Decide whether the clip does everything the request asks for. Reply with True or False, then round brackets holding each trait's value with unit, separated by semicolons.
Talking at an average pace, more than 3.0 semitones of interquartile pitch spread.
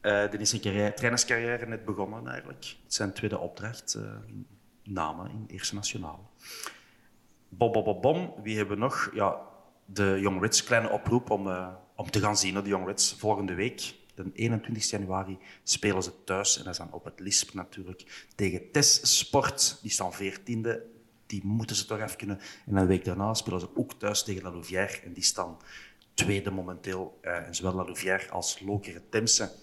False (190 wpm; 2.7 semitones)